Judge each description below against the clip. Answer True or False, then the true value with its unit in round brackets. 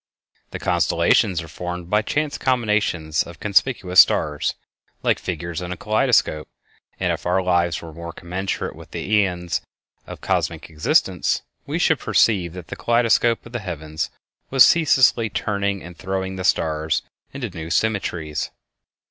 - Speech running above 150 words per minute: False (145 wpm)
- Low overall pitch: True (90 Hz)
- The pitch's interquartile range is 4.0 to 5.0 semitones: True (4.3 semitones)